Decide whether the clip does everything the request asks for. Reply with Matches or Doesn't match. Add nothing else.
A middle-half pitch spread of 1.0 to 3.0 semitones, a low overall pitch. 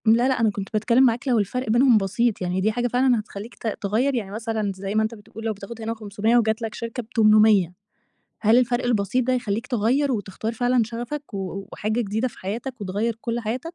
Doesn't match